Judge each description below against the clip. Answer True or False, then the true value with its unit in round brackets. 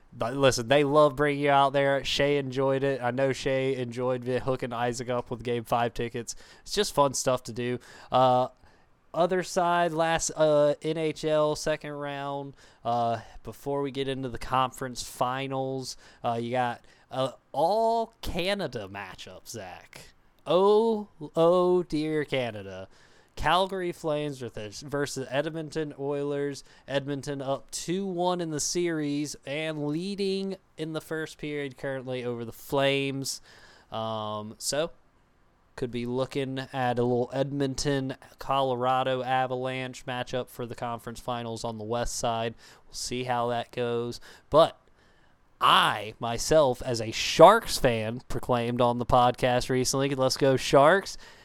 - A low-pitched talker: True (130 Hz)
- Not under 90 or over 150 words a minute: True (140 wpm)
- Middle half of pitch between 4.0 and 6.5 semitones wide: False (3.4 semitones)